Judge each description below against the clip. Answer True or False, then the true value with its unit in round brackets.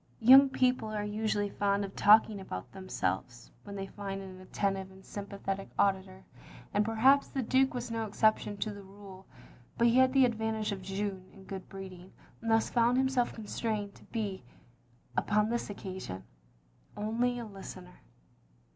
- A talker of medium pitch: False (205 Hz)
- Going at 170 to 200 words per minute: False (160 wpm)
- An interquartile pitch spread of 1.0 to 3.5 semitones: True (2.8 semitones)